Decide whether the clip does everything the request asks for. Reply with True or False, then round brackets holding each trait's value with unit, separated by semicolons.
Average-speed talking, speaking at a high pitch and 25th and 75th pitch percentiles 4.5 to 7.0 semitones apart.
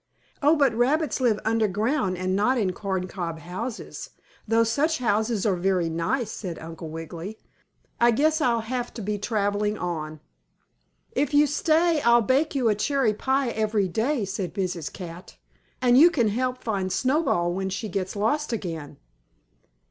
True (155 wpm; 215 Hz; 5.5 semitones)